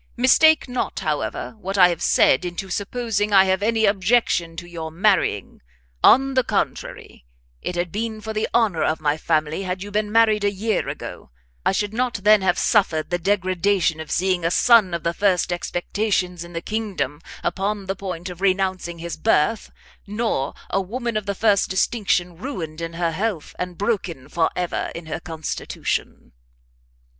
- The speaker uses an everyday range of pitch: Yes, average, 3.8 semitones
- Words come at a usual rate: Yes, average, 175 wpm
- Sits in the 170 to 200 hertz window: Yes, high, 190 Hz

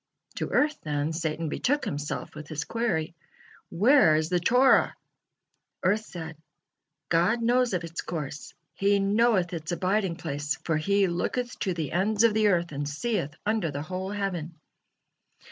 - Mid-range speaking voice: Yes, medium, 175 Hz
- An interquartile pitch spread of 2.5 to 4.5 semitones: No, average, 5.3 semitones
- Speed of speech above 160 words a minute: No, average, 155 wpm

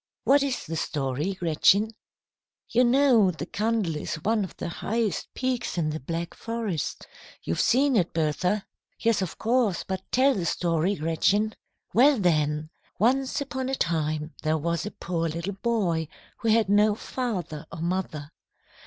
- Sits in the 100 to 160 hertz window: No, high, 190 Hz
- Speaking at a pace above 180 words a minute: No, average, 155 wpm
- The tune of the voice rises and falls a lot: Yes, wide, 6.0 semitones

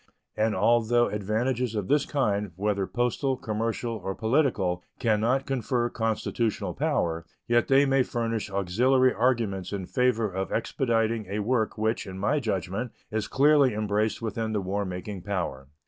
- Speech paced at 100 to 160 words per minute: Yes, average, 150 wpm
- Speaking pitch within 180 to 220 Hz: No, low, 110 Hz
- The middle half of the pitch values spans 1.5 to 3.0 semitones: No, average, 3.5 semitones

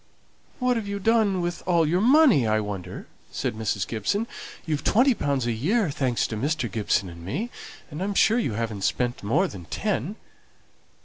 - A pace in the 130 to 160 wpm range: No, average, 180 wpm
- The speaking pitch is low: No, medium, 155 Hz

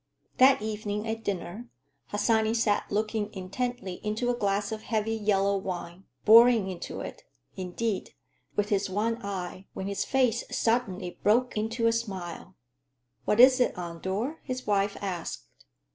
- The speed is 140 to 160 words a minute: Yes, average, 145 wpm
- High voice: Yes, high, 210 Hz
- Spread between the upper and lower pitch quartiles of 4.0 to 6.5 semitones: No, average, 3.0 semitones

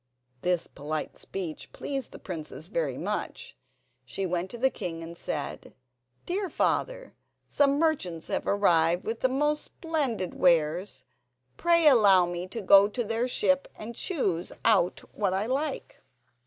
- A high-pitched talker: Yes, high, 205 Hz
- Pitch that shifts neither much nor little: No, wide, 7.9 semitones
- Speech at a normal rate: Yes, average, 145 wpm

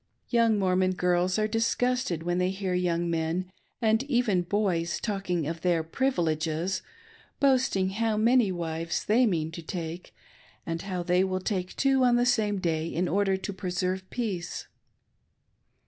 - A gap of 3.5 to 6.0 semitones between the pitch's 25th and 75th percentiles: Yes, average, 3.9 semitones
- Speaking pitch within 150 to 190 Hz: Yes, medium, 185 Hz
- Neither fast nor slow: Yes, average, 160 wpm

